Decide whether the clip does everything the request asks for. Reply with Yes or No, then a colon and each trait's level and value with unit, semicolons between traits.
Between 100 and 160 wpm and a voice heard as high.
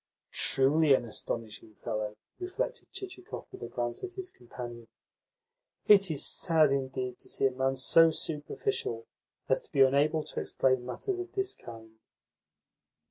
No: average, 145 wpm; low, 135 Hz